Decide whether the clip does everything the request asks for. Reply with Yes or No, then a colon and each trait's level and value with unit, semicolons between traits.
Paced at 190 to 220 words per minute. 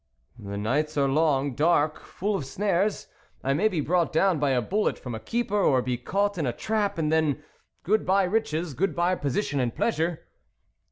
Yes: average, 200 wpm